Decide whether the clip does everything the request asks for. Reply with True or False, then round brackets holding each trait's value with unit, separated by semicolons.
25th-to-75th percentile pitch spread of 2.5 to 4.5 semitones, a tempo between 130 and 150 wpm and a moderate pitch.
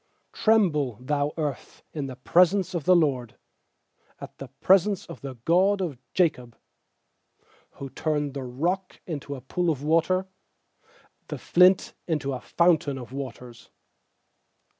False (5.1 semitones; 140 wpm; 150 Hz)